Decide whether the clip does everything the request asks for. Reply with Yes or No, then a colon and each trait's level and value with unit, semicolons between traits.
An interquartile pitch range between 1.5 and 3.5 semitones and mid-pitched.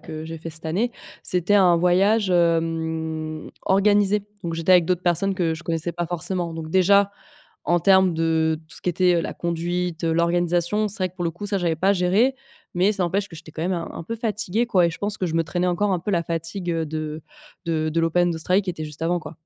Yes: narrow, 2.5 semitones; medium, 175 Hz